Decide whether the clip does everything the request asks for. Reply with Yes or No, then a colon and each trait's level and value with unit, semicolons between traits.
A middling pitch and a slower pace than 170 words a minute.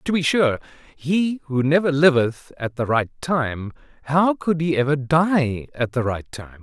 No: medium, 145 Hz; average, 180 wpm